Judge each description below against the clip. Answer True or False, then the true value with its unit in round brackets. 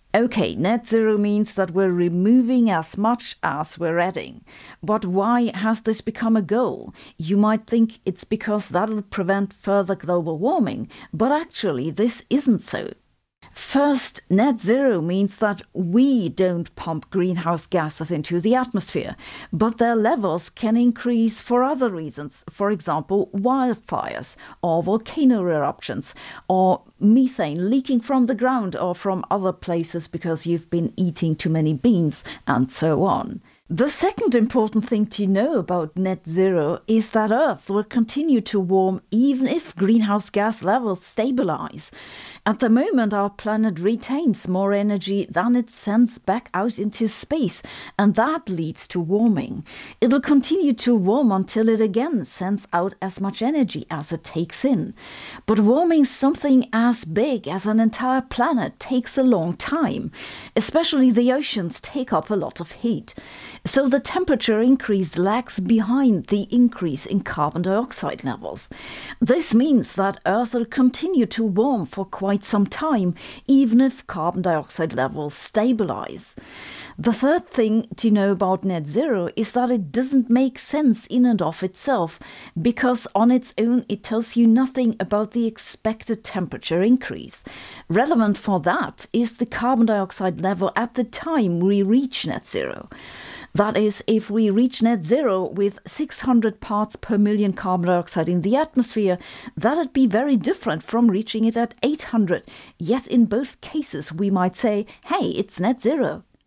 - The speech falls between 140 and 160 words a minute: True (155 wpm)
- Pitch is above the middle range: True (220 Hz)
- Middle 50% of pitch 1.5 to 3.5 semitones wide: False (4.4 semitones)